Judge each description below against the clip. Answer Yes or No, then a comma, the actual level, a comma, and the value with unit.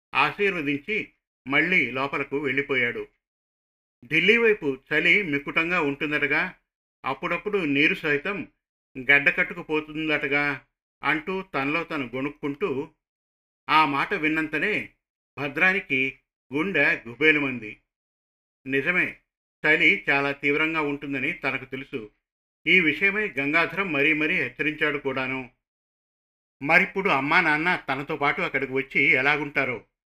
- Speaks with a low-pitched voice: No, medium, 145 Hz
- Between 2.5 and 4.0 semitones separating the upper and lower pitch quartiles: Yes, average, 2.8 semitones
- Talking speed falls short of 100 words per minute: Yes, average, 90 wpm